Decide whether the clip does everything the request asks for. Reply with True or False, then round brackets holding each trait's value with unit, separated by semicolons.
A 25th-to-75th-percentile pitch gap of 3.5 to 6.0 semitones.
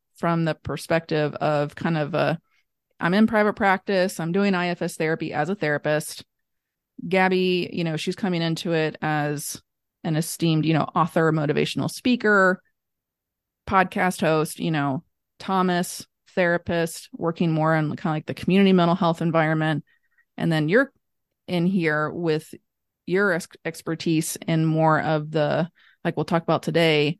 False (2.8 semitones)